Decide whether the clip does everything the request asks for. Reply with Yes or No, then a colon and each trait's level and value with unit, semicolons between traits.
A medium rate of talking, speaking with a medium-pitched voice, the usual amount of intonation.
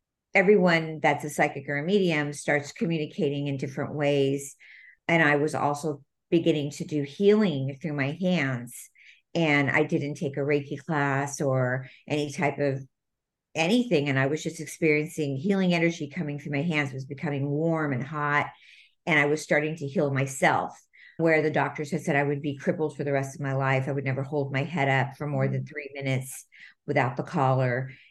No: average, 190 wpm; medium, 145 Hz; narrow, 2.2 semitones